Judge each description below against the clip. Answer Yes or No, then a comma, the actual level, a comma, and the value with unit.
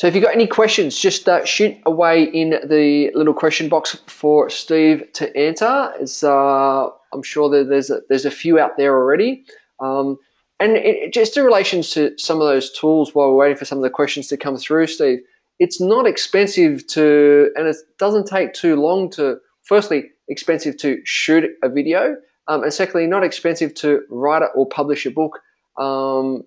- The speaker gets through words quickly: No, average, 190 wpm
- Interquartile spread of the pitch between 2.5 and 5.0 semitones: No, wide, 5.4 semitones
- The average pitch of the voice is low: No, medium, 155 Hz